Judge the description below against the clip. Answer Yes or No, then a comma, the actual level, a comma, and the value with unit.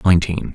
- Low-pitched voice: Yes, very low, 85 Hz